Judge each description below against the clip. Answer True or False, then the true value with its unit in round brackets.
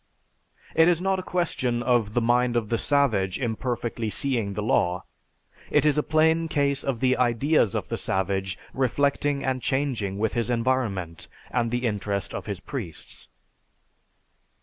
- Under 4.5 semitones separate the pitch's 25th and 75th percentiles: False (4.9 semitones)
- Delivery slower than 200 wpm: True (155 wpm)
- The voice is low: True (120 Hz)